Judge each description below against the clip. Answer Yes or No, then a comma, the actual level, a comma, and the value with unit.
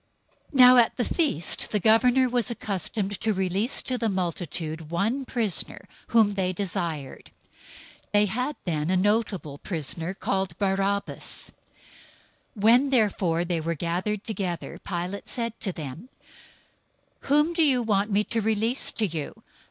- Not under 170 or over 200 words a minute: No, average, 145 wpm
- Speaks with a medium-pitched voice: No, high, 200 Hz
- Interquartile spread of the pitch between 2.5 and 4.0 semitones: No, average, 4.8 semitones